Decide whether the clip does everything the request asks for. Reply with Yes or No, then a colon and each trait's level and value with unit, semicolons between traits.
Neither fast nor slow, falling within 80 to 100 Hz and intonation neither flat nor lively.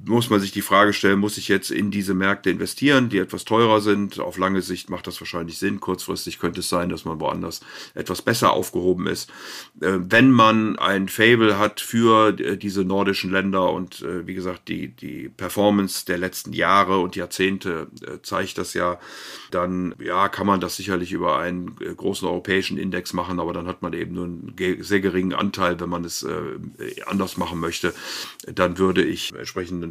No: average, 180 wpm; very low, 95 Hz; narrow, 2.1 semitones